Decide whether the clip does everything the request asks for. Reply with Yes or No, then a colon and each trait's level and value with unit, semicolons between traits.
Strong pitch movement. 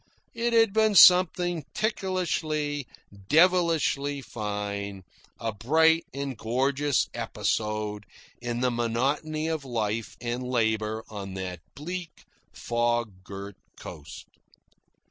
Yes: wide, 7.0 semitones